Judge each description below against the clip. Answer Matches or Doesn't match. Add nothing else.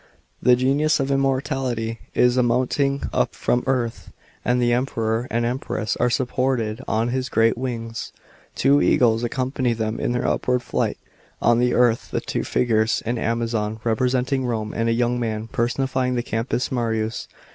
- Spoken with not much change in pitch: Matches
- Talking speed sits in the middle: Matches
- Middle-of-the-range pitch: Doesn't match